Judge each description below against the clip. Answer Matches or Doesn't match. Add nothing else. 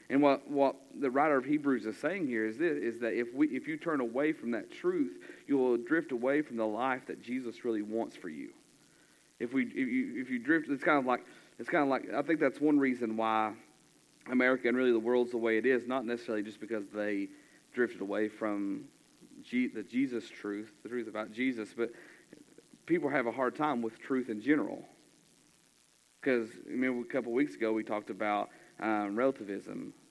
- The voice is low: Matches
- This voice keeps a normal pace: Doesn't match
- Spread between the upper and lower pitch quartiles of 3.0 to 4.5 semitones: Doesn't match